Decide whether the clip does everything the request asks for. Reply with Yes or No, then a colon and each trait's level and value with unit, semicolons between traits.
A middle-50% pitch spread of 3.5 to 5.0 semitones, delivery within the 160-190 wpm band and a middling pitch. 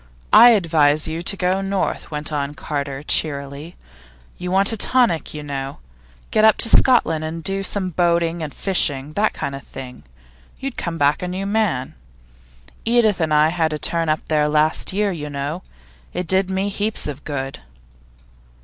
Yes: average, 4.6 semitones; average, 175 wpm; medium, 165 Hz